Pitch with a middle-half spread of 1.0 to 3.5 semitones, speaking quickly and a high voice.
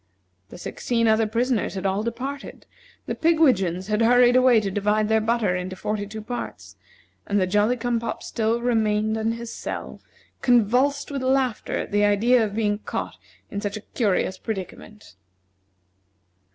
No: average, 2.8 semitones; average, 160 wpm; high, 220 Hz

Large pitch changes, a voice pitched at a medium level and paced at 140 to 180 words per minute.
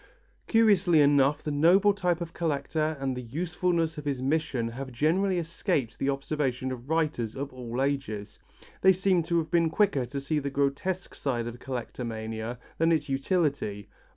No: average, 4.5 semitones; medium, 145 Hz; average, 165 wpm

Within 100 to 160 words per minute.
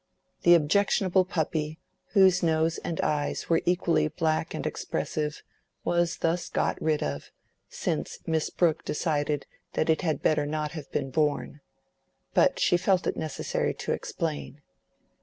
Yes: average, 140 wpm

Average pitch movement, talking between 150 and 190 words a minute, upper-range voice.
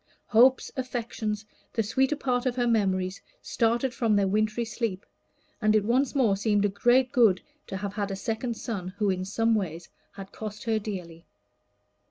Yes: average, 3.3 semitones; average, 175 wpm; high, 215 Hz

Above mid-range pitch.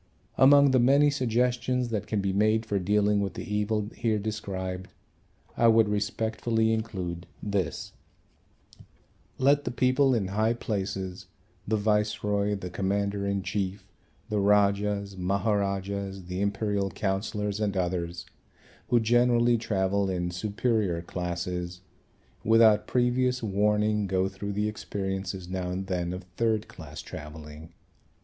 No: low, 100 Hz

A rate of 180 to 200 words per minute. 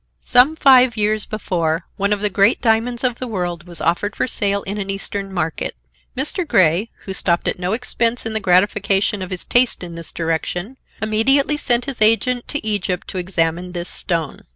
Yes: average, 190 wpm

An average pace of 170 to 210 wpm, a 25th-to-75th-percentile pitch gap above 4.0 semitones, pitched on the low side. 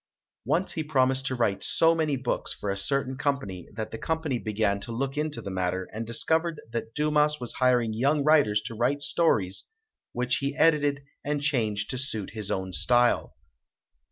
Yes: average, 180 wpm; average, 5.3 semitones; low, 130 Hz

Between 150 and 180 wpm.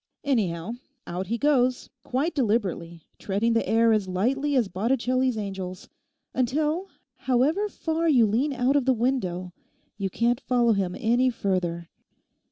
No: average, 140 wpm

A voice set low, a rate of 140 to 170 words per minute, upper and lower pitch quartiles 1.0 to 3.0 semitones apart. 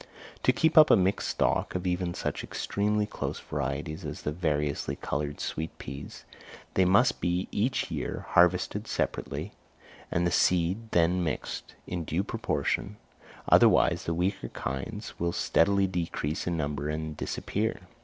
No: very low, 85 Hz; average, 145 wpm; average, 4.1 semitones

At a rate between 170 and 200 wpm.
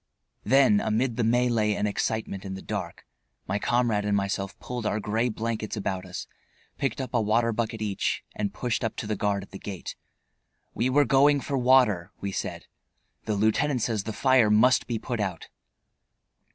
Yes: average, 180 wpm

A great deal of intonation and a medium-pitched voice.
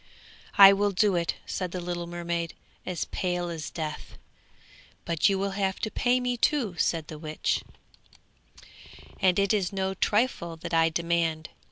No: average, 2.9 semitones; medium, 180 Hz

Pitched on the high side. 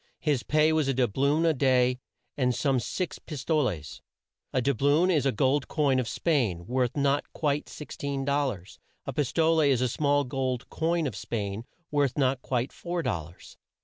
No: low, 135 Hz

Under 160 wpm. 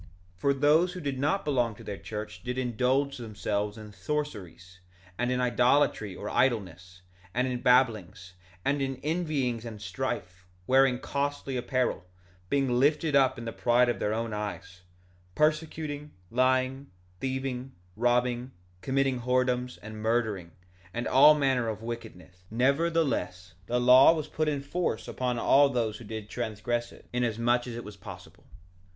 Yes: average, 150 wpm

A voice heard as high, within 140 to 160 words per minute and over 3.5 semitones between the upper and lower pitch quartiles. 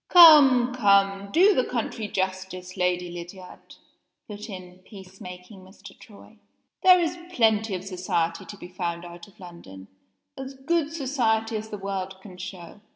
Yes: high, 195 Hz; average, 155 wpm; average, 4.1 semitones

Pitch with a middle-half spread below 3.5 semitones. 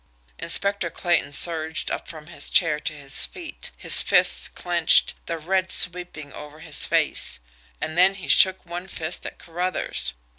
Yes: average, 2.7 semitones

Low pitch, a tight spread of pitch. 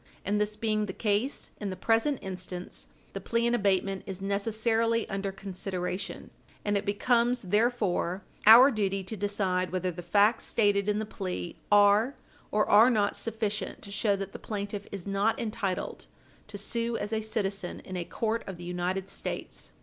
No: high, 205 Hz; narrow, 2.3 semitones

